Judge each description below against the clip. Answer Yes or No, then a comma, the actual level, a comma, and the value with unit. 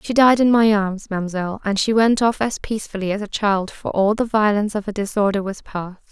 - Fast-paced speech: Yes, fast, 235 wpm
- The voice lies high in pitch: Yes, high, 205 Hz